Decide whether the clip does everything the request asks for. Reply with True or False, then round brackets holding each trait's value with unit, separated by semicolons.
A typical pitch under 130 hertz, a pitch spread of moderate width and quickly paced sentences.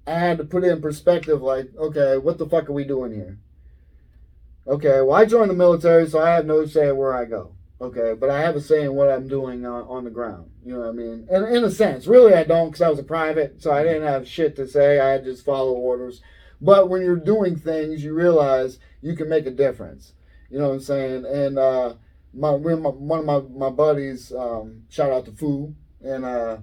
False (140 Hz; 4.2 semitones; 235 wpm)